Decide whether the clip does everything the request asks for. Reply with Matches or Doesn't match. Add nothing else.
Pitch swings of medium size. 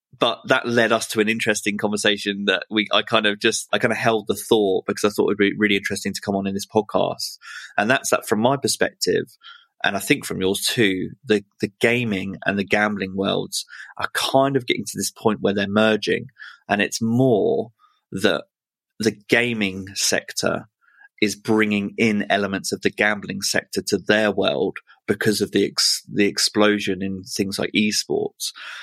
Doesn't match